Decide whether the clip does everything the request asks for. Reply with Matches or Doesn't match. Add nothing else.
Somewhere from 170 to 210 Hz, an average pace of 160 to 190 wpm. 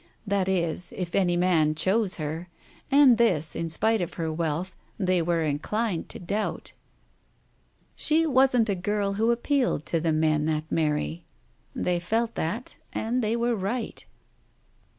Doesn't match